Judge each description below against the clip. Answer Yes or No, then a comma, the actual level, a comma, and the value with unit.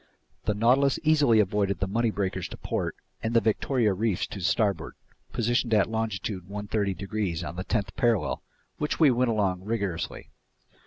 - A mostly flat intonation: No, average, 3.1 semitones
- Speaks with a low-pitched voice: Yes, low, 105 Hz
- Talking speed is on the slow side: No, average, 160 wpm